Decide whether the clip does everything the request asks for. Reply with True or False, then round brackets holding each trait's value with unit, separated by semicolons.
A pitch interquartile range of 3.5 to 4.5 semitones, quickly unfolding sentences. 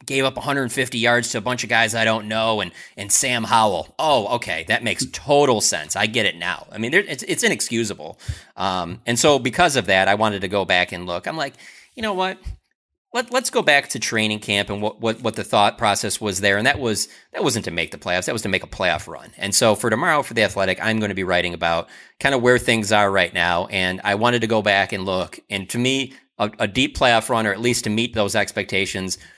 True (4.0 semitones; 255 wpm)